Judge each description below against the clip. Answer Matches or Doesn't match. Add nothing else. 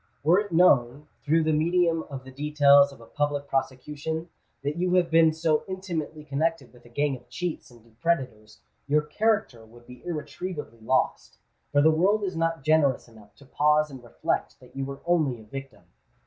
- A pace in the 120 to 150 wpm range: Doesn't match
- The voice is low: Doesn't match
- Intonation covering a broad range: Doesn't match